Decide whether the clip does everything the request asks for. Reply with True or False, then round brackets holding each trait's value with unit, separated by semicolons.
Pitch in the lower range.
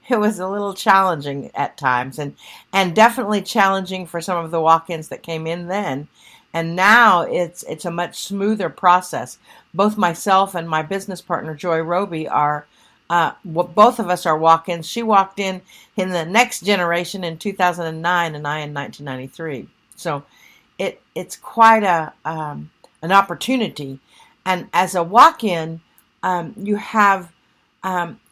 False (175 Hz)